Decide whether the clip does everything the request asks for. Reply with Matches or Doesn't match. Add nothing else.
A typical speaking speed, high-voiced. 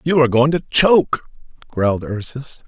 Doesn't match